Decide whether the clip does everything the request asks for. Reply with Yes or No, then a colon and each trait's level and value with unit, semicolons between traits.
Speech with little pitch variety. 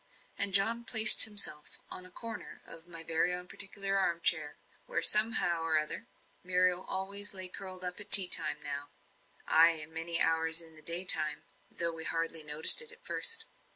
No: average, 3.4 semitones